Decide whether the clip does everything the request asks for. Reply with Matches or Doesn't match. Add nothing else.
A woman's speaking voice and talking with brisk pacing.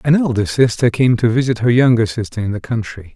Doesn't match